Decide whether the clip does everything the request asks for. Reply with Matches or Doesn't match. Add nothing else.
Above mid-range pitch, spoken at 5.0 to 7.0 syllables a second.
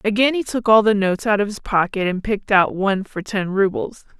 Matches